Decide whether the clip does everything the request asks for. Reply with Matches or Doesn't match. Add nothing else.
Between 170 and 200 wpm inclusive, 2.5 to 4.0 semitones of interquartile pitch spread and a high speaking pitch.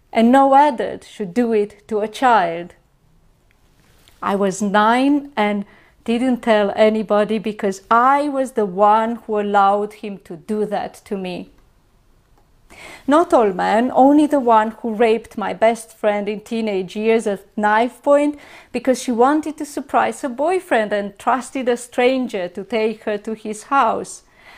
Doesn't match